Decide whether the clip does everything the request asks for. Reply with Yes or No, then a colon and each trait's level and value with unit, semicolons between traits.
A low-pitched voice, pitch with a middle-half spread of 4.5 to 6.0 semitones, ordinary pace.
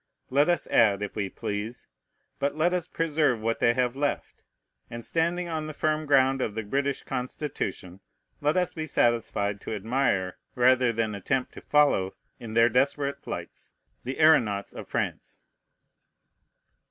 Yes: low, 130 Hz; average, 5.1 semitones; average, 155 wpm